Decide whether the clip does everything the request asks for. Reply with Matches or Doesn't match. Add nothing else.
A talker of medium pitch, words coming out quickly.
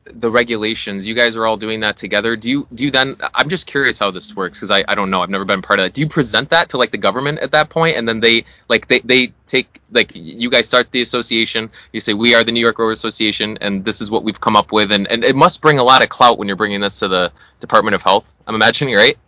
Doesn't match